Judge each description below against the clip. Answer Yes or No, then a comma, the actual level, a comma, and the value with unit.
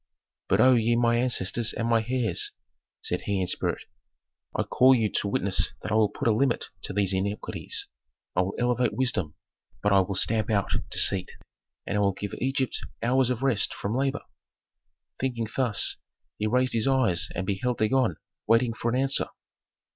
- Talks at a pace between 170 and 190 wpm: Yes, average, 175 wpm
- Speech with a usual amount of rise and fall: Yes, average, 3.9 semitones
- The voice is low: Yes, low, 115 Hz